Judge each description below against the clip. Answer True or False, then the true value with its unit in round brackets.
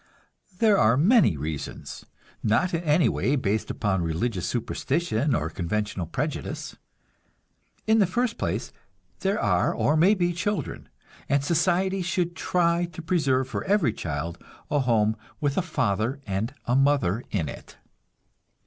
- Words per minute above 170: False (140 wpm)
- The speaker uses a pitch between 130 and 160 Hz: True (140 Hz)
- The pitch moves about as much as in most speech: False (8.5 semitones)